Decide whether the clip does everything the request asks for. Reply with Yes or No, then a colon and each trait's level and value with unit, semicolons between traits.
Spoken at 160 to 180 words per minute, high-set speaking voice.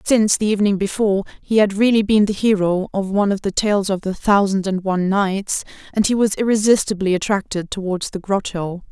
No: average, 195 wpm; high, 200 Hz